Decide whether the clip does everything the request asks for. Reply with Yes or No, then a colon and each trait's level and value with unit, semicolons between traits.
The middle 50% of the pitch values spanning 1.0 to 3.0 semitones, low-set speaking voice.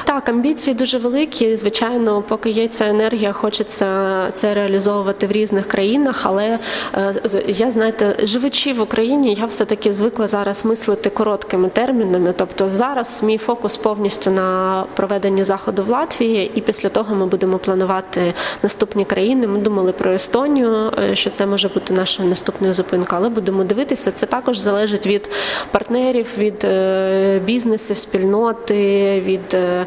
No: narrow, 2.6 semitones; high, 205 Hz